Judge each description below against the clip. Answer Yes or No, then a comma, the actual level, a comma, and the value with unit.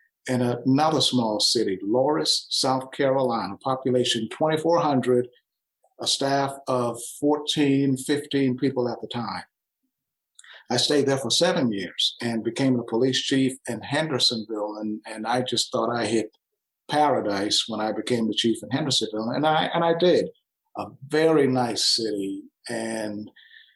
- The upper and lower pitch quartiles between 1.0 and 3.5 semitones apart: No, average, 3.9 semitones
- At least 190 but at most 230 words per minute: No, average, 140 wpm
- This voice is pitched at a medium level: No, low, 125 Hz